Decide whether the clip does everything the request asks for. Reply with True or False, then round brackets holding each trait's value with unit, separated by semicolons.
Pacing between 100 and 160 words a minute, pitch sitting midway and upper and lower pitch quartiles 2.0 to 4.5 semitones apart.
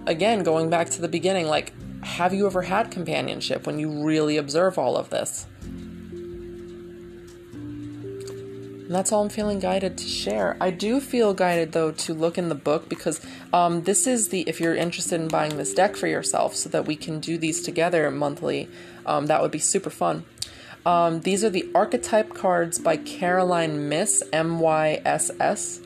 False (180 wpm; 170 Hz; 2.9 semitones)